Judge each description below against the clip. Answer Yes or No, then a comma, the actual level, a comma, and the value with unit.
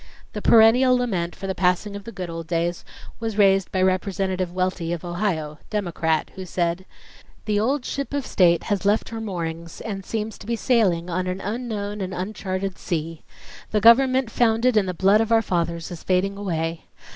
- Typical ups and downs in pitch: Yes, average, 4.1 semitones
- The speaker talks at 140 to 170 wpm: No, average, 185 wpm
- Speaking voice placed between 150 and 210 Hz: Yes, high, 190 Hz